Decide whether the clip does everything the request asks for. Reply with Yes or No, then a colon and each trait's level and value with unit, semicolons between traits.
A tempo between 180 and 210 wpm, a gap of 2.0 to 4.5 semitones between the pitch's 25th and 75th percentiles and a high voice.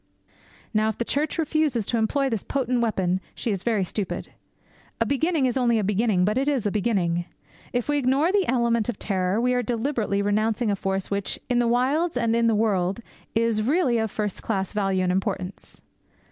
Yes: average, 200 wpm; average, 3.8 semitones; high, 225 Hz